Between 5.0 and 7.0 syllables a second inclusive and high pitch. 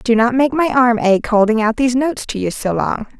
Yes: 5.6 syllables/s; high, 240 Hz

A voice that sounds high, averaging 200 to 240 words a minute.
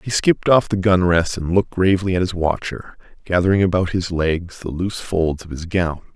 No: very low, 90 Hz; fast, 205 wpm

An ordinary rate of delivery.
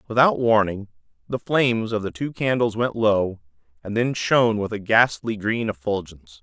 Yes: average, 170 wpm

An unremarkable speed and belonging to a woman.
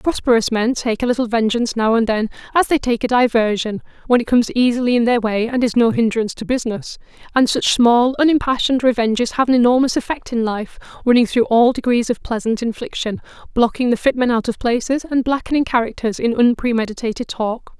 Yes: average, 195 wpm; female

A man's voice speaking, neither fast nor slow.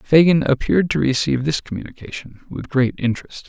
Yes: male; average, 155 wpm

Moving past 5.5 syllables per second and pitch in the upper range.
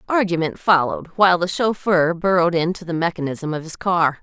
No: 5.8 syllables/s; medium, 175 Hz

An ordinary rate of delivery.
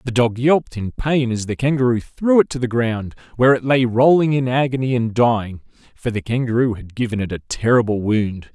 No: fast, 210 wpm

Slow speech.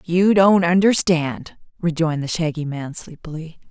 Yes: slow, 130 wpm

